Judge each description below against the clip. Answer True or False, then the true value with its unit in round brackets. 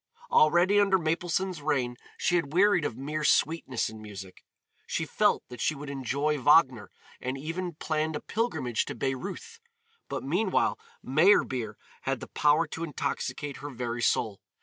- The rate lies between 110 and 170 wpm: True (150 wpm)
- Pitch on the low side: False (150 Hz)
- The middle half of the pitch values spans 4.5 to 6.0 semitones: True (5.1 semitones)